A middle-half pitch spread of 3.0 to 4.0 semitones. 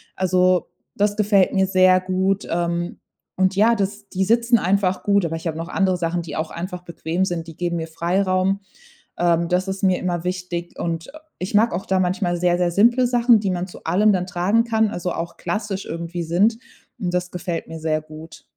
No: narrow, 2.5 semitones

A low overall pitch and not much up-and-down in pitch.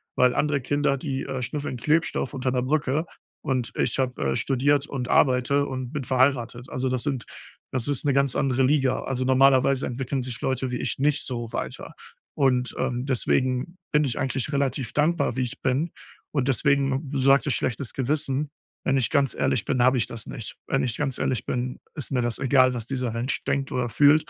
Yes: low, 130 Hz; narrow, 1.9 semitones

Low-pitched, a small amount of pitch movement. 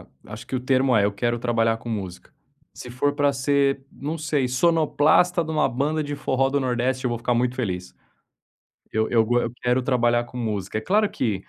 No: low, 125 Hz; average, 3.4 semitones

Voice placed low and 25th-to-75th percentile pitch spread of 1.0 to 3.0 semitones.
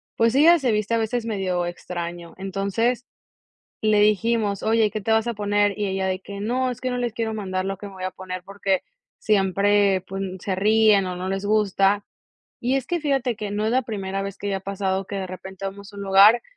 No: high, 200 Hz; narrow, 2.5 semitones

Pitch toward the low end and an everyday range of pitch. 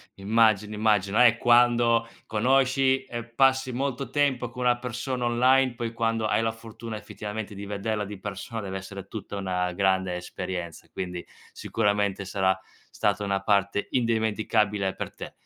Yes: low, 110 Hz; average, 3.4 semitones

